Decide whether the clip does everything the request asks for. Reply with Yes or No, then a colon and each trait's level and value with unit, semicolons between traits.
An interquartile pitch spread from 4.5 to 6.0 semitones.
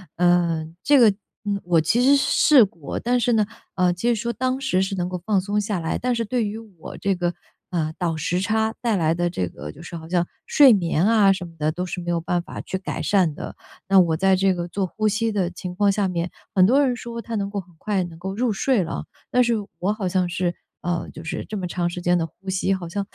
No: average, 3.7 semitones